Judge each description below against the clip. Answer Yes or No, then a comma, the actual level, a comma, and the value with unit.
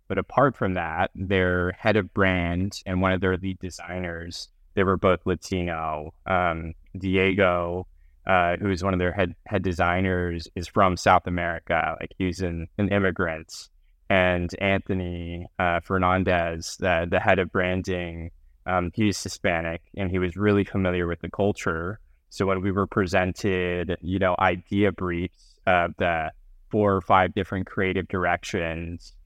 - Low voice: Yes, very low, 90 Hz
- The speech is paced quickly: No, average, 155 wpm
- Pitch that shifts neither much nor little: No, narrow, 1.9 semitones